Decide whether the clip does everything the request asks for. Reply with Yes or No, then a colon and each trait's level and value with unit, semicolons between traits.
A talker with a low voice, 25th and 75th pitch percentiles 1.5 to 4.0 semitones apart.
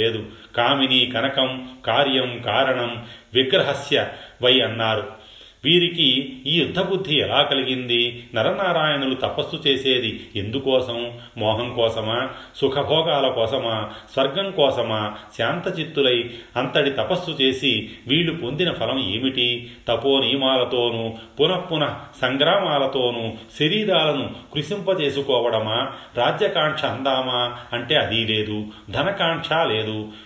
Yes: low, 130 Hz; average, 3.7 semitones